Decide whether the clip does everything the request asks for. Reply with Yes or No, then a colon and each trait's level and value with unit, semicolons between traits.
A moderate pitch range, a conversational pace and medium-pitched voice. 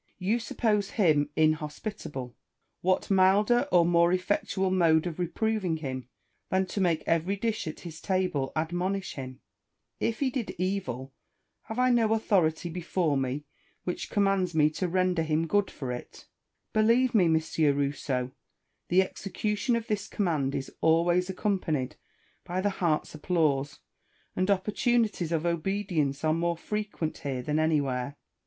Yes: average, 4.4 semitones; average, 145 wpm; medium, 175 Hz